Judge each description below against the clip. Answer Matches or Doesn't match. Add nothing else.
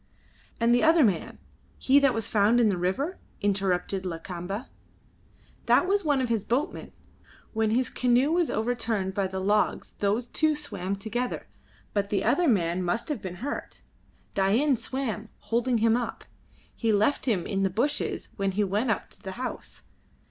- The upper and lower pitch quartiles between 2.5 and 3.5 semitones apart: Doesn't match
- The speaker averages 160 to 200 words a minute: Matches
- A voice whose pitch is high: Matches